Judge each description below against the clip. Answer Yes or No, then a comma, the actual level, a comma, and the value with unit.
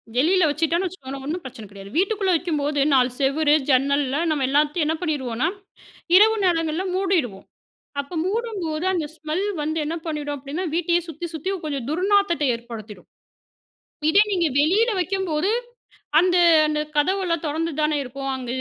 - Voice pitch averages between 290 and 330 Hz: Yes, very high, 310 Hz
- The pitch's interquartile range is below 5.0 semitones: Yes, average, 4.5 semitones